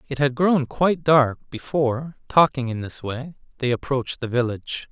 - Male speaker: Yes, male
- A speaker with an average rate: Yes, average, 170 wpm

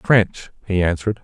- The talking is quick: No, average, 145 wpm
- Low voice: Yes, very low, 95 Hz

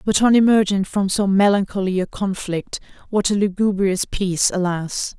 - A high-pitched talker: Yes, high, 195 Hz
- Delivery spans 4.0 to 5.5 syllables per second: Yes, 4.8 syllables/s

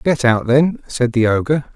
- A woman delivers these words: No, male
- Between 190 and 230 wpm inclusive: Yes, fast, 205 wpm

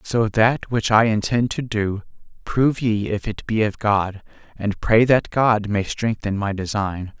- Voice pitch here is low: Yes, low, 105 Hz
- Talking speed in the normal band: Yes, average, 185 wpm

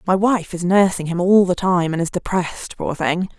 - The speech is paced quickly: Yes, fast, 230 wpm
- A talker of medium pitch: Yes, medium, 180 Hz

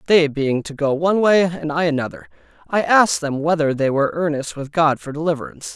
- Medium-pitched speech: Yes, medium, 155 Hz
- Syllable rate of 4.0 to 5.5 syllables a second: No, 6.0 syllables/s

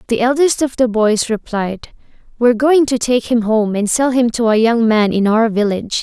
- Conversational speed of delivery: No, fast, 220 wpm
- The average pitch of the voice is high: Yes, high, 230 Hz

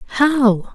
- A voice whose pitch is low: No, high, 245 Hz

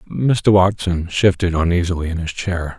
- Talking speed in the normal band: Yes, average, 150 wpm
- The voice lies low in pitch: Yes, very low, 90 Hz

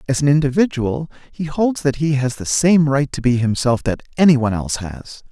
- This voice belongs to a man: Yes, male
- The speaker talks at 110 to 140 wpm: No, fast, 205 wpm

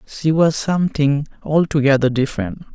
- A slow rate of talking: Yes, slow, 110 wpm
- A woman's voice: No, male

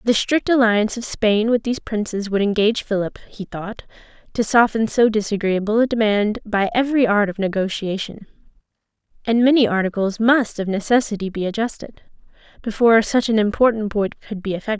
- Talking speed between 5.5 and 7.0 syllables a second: Yes, 5.7 syllables/s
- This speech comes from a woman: Yes, female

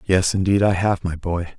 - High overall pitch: No, very low, 95 Hz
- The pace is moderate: No, fast, 230 wpm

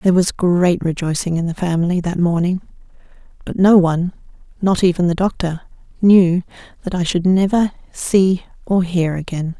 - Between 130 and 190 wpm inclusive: Yes, average, 155 wpm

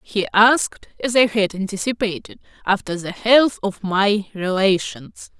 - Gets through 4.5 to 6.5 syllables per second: No, 4.3 syllables/s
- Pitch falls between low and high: No, high, 205 Hz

